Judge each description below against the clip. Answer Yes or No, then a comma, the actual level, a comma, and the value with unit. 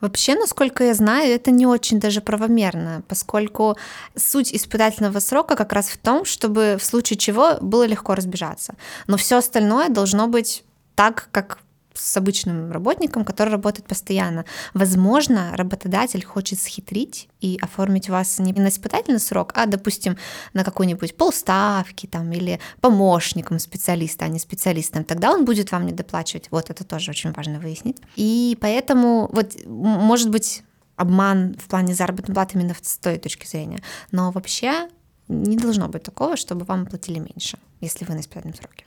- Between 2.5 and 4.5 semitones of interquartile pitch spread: Yes, average, 3.8 semitones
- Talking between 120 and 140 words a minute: No, fast, 160 wpm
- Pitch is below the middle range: No, high, 200 Hz